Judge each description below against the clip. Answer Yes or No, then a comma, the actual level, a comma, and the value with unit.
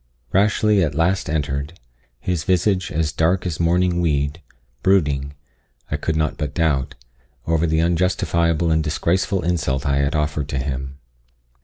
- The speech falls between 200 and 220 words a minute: No, average, 145 wpm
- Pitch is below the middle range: Yes, very low, 80 Hz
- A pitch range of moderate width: Yes, average, 3.4 semitones